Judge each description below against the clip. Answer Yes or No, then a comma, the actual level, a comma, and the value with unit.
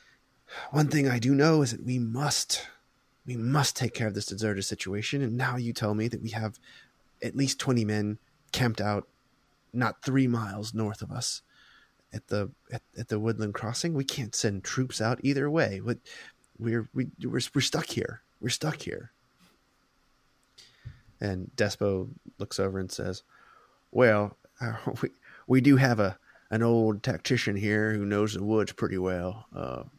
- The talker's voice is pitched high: No, low, 115 Hz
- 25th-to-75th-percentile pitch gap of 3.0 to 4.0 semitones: Yes, average, 3.5 semitones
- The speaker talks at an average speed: Yes, average, 170 wpm